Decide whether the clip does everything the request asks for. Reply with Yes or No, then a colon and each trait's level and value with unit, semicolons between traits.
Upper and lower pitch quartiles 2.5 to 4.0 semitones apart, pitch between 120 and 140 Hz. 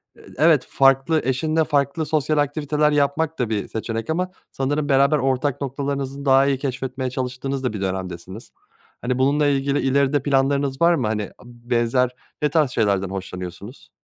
Yes: average, 2.8 semitones; low, 135 Hz